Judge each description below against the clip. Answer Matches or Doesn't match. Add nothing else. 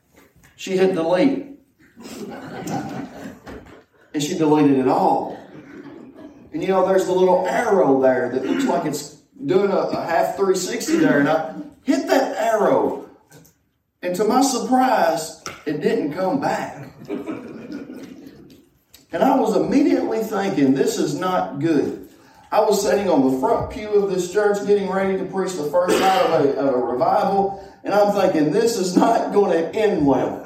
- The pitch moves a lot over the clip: Matches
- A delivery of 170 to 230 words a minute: Doesn't match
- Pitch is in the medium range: Doesn't match